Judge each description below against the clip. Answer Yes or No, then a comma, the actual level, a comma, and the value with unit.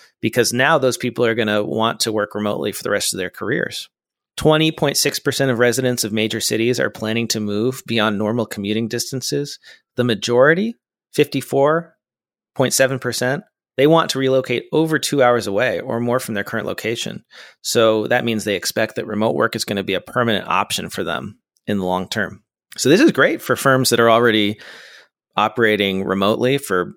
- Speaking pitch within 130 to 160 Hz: No, low, 120 Hz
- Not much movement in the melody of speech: No, average, 3.5 semitones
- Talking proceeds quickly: No, average, 180 wpm